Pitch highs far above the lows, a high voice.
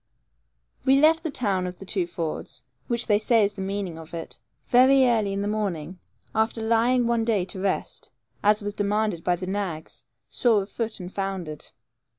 No: average, 3.7 semitones; high, 205 Hz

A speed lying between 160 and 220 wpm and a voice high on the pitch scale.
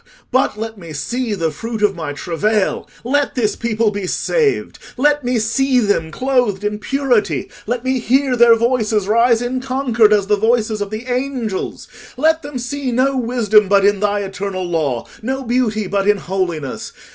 Yes: average, 170 wpm; high, 225 Hz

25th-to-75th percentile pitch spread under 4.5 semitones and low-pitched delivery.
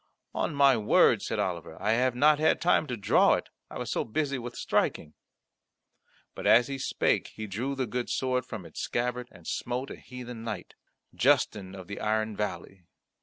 Yes: average, 3.7 semitones; low, 120 Hz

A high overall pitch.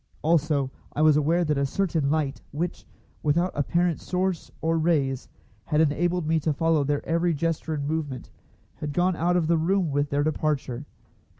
No: medium, 155 Hz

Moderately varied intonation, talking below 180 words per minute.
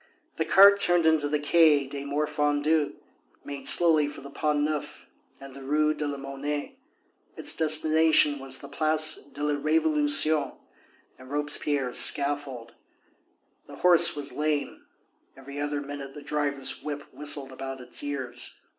No: narrow, 1.6 semitones; average, 145 wpm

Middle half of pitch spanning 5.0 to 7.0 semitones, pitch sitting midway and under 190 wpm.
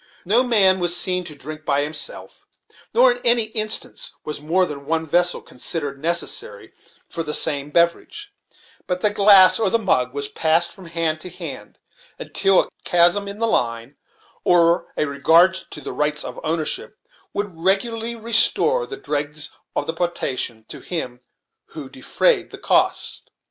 Yes: average, 5.3 semitones; medium, 175 Hz; average, 165 wpm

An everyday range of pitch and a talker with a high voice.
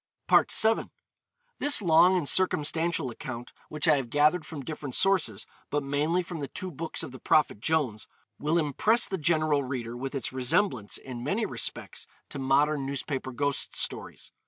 No: average, 4.1 semitones; medium, 145 Hz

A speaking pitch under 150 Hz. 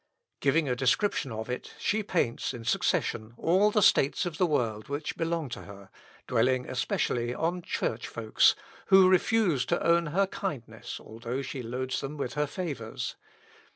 Yes: medium, 140 Hz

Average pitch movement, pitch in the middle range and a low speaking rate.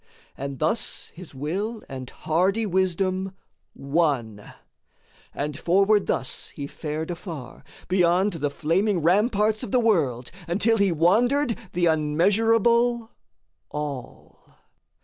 No: wide, 5.8 semitones; medium, 180 Hz; slow, 110 wpm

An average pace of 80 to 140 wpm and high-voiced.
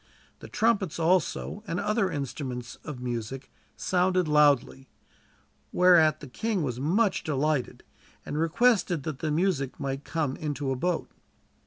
No: slow, 135 wpm; medium, 155 Hz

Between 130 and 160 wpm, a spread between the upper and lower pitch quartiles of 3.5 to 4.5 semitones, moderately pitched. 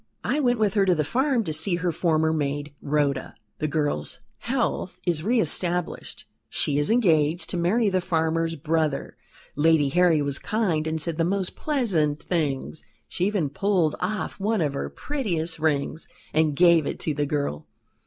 No: average, 175 wpm; average, 4.0 semitones; medium, 165 Hz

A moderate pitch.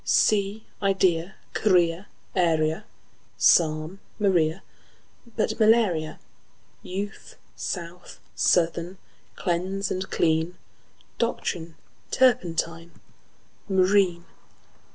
Yes: medium, 180 Hz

